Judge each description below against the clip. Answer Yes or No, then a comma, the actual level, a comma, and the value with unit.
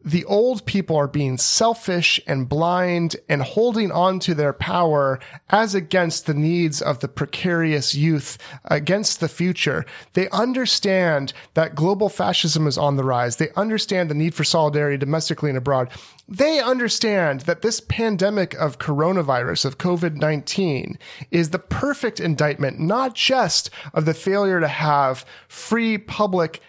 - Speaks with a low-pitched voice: No, medium, 170 Hz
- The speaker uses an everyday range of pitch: Yes, average, 4.8 semitones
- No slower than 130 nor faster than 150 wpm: Yes, average, 145 wpm